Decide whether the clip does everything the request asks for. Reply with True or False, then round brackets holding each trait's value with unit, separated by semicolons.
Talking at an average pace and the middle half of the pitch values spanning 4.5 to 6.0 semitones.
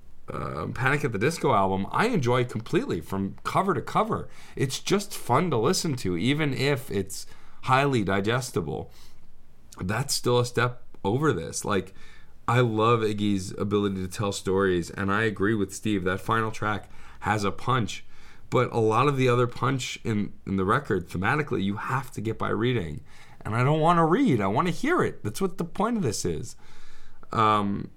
True (195 wpm; 4.9 semitones)